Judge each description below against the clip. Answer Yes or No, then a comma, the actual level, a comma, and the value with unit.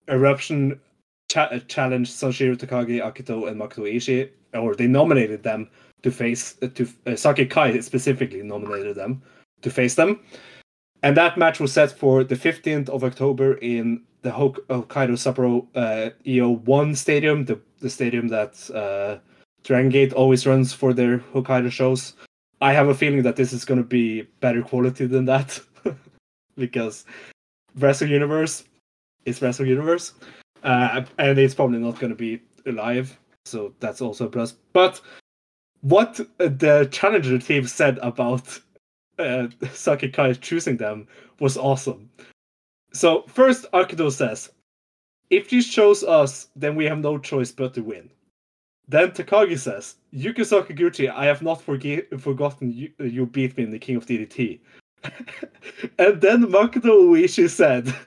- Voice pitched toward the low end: Yes, low, 130 Hz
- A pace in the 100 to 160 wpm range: Yes, average, 150 wpm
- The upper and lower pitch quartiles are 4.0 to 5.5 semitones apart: No, average, 2.9 semitones